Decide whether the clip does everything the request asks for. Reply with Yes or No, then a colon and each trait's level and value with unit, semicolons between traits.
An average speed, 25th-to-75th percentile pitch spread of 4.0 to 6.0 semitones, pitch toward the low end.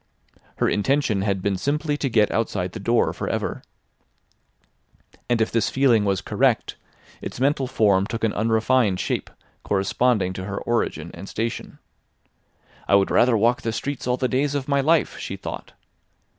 Yes: average, 165 wpm; average, 4.5 semitones; low, 115 Hz